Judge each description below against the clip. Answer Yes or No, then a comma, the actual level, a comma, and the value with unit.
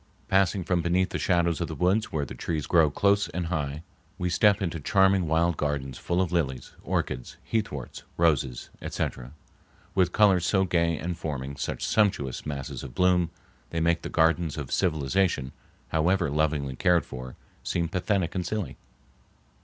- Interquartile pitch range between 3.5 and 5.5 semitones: Yes, average, 3.9 semitones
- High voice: No, very low, 85 Hz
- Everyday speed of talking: Yes, average, 160 wpm